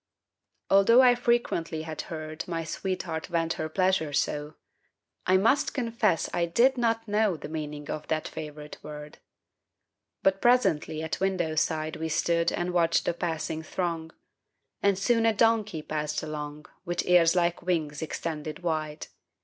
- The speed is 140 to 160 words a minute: Yes, average, 150 wpm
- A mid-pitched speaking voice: Yes, medium, 165 Hz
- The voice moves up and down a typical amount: Yes, average, 3.6 semitones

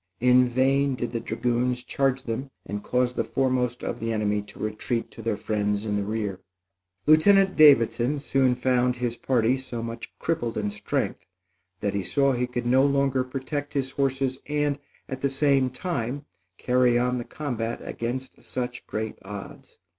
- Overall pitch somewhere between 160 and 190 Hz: No, low, 125 Hz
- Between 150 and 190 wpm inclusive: Yes, average, 170 wpm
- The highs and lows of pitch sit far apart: No, average, 2.9 semitones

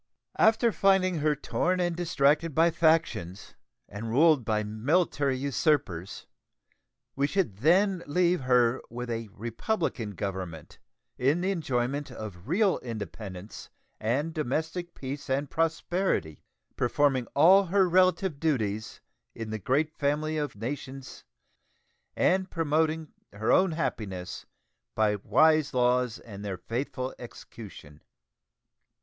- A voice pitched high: No, medium, 140 Hz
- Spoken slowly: Yes, slow, 115 wpm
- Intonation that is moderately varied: No, wide, 6.7 semitones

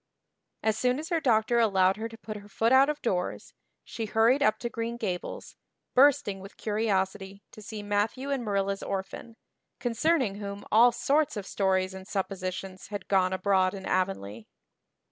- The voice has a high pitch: Yes, high, 210 Hz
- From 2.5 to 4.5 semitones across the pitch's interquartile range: Yes, average, 3.5 semitones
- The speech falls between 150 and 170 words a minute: Yes, average, 165 wpm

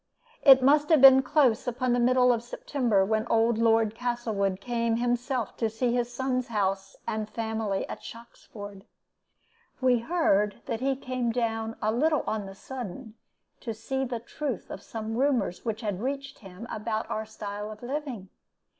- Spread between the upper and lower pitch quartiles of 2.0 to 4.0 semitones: Yes, average, 2.8 semitones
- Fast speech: No, average, 170 wpm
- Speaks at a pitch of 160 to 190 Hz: No, high, 230 Hz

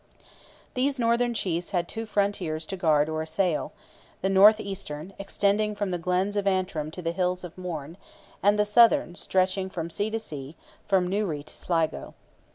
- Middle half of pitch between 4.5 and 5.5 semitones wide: No, average, 3.7 semitones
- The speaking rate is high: No, average, 175 wpm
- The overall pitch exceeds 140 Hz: Yes, medium, 185 Hz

